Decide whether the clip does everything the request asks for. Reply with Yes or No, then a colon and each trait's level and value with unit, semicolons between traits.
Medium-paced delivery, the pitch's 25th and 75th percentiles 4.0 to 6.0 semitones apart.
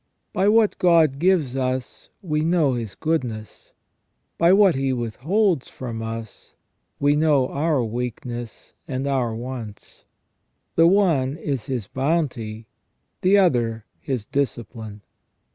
No: slow, 120 wpm; wide, 5.6 semitones